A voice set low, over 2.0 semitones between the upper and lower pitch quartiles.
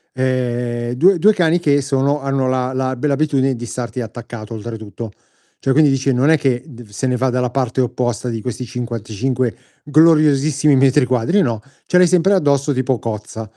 Yes: low, 130 Hz; average, 2.9 semitones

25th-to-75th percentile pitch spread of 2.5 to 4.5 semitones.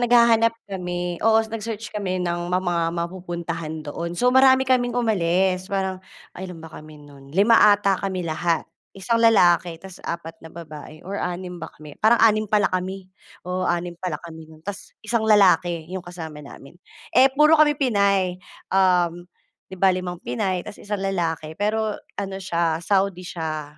Yes: average, 3.6 semitones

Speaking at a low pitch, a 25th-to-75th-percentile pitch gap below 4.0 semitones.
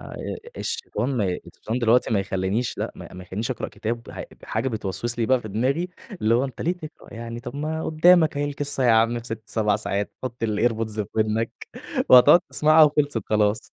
No: low, 115 Hz; average, 4.6 semitones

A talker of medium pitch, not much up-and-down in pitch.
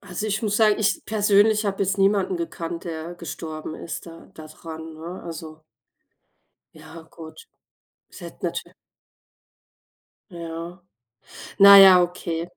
No: medium, 175 Hz; average, 3.5 semitones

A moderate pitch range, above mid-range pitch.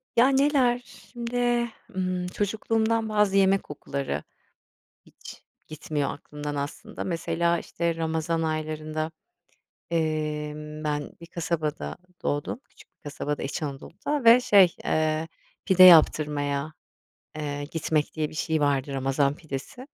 No: average, 4.6 semitones; medium, 160 Hz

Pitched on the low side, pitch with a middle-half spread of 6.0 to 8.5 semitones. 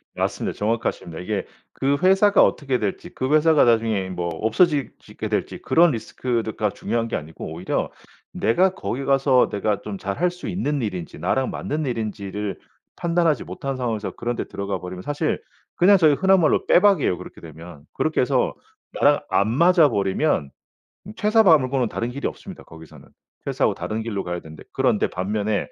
Yes: low, 120 Hz; wide, 7.5 semitones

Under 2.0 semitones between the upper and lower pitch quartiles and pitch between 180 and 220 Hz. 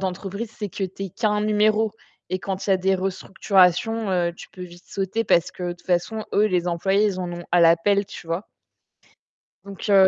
No: average, 2.7 semitones; high, 190 Hz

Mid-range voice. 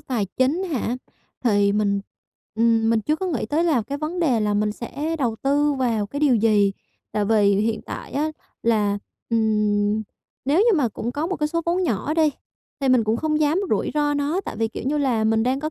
No: very high, 250 Hz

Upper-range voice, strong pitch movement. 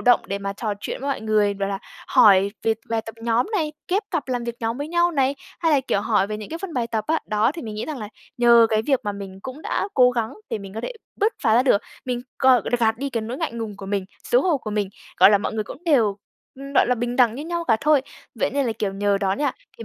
No: high, 235 Hz; average, 4.8 semitones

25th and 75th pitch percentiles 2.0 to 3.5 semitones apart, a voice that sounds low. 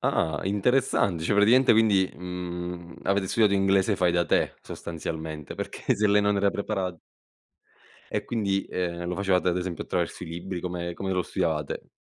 Yes: narrow, 2.5 semitones; very low, 90 Hz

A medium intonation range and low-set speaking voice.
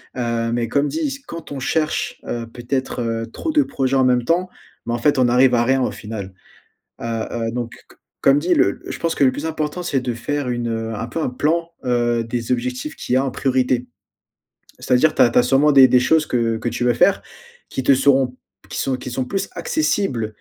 Yes: average, 3.6 semitones; low, 125 Hz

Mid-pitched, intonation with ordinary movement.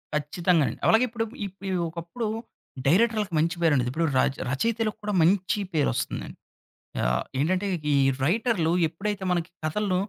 Yes: medium, 180 Hz; average, 4.7 semitones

